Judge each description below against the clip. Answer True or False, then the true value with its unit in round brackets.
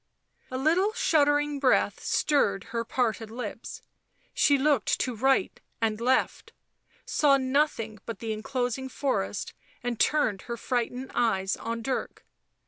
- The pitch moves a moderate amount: True (3.7 semitones)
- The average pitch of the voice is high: True (250 Hz)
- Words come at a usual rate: False (130 wpm)